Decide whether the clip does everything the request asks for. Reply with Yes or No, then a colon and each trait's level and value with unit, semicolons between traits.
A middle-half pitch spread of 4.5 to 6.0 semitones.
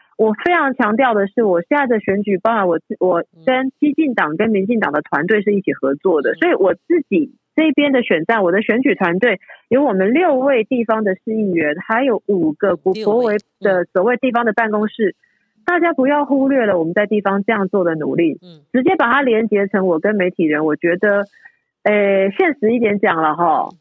Yes: wide, 5.5 semitones